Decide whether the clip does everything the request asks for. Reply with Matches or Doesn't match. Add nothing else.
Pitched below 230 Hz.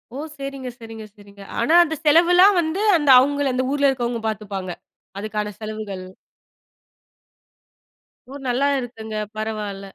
Doesn't match